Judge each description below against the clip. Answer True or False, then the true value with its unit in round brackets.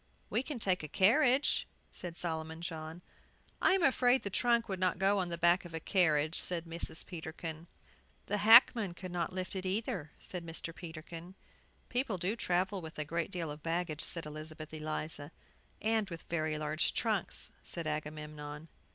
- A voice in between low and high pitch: True (170 Hz)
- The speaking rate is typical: True (170 wpm)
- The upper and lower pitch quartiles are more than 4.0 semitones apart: False (3.5 semitones)